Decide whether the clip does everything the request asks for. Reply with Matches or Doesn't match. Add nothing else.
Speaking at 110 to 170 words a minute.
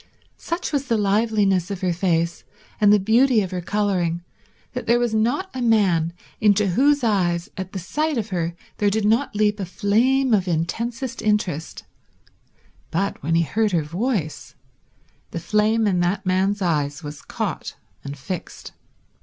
Matches